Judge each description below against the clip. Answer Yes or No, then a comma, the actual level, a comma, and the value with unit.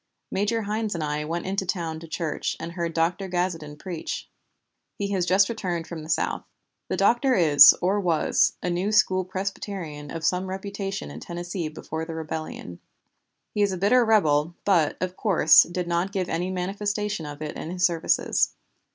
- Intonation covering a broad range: No, average, 3.5 semitones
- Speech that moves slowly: No, average, 175 wpm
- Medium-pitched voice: Yes, medium, 180 Hz